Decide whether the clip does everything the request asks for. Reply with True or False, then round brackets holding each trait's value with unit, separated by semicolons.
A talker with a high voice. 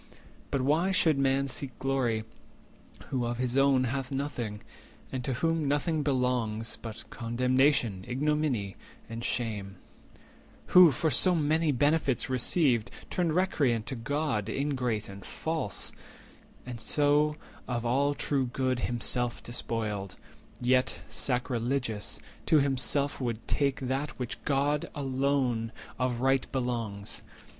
False (130 Hz)